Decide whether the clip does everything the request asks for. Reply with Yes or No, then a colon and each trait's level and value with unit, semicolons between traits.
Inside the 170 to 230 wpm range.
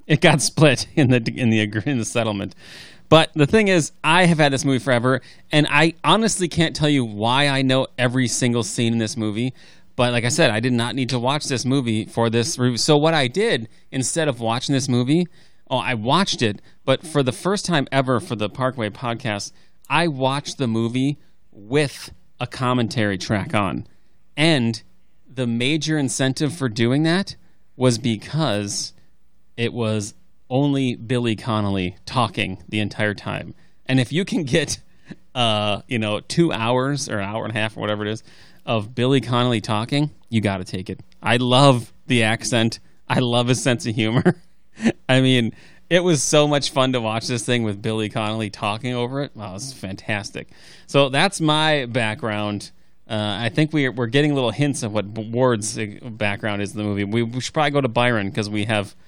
Yes: average, 190 wpm